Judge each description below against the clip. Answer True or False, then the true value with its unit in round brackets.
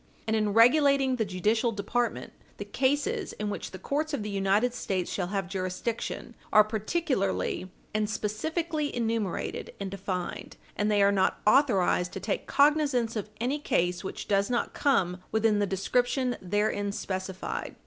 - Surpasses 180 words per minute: False (155 wpm)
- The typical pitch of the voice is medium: False (215 Hz)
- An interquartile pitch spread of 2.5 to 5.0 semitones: True (4.3 semitones)